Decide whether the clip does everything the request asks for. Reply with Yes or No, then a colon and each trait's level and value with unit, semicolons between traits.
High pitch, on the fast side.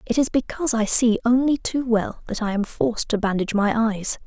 Yes: high, 230 Hz; fast, 225 wpm